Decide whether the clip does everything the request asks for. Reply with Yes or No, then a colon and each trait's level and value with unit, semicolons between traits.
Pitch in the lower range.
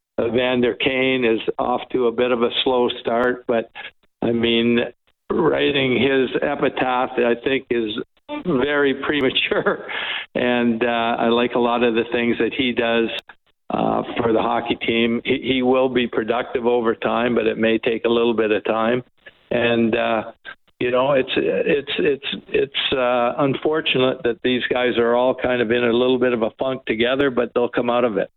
Yes: low, 120 Hz